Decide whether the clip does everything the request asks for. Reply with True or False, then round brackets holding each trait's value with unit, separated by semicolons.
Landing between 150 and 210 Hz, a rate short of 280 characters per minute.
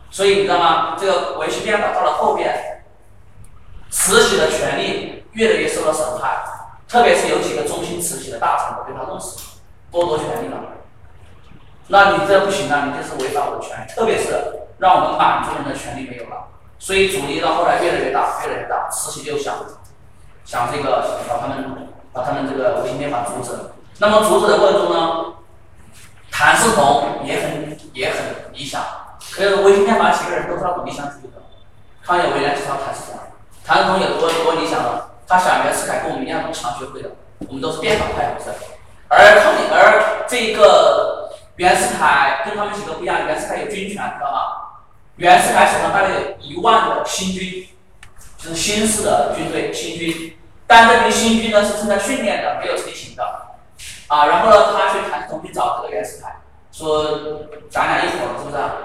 False (185 Hz; 290 characters per minute)